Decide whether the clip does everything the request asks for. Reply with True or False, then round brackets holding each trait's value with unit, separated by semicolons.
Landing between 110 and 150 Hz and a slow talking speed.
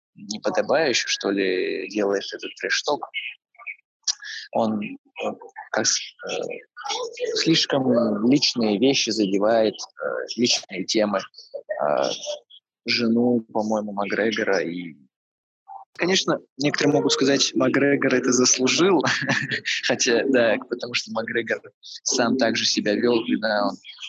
True (135 Hz; 90 wpm)